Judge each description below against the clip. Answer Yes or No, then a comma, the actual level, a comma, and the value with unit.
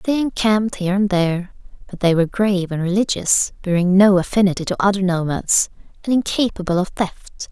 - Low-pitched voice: No, high, 190 Hz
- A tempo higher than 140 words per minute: Yes, average, 170 wpm